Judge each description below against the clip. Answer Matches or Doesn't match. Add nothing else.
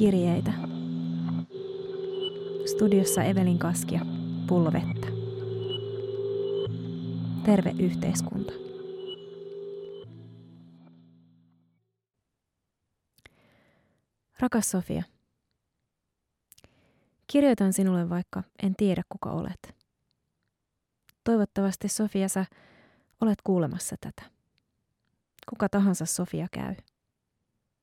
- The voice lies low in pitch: Doesn't match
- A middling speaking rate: Doesn't match